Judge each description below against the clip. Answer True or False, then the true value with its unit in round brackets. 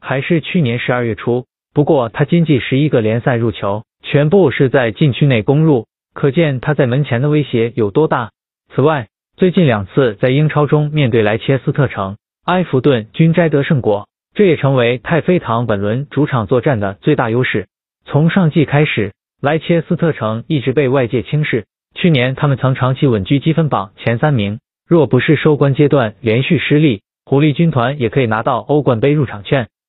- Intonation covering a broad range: False (4.5 semitones)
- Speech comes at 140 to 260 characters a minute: False (285 characters per minute)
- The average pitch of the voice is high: False (140 Hz)